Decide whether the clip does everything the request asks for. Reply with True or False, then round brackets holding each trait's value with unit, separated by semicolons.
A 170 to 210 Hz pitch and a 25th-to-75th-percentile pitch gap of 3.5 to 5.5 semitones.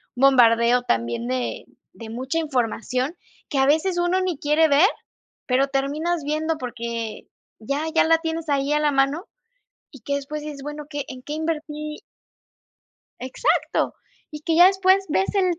False (290 Hz; 4.0 semitones)